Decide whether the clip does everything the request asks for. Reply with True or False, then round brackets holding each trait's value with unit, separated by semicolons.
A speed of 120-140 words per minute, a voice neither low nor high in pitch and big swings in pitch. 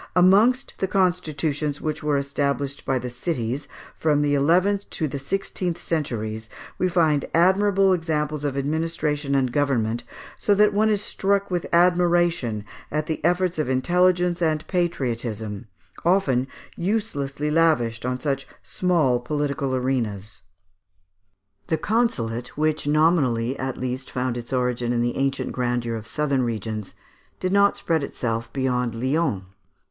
True (135 wpm; 145 Hz; 5.7 semitones)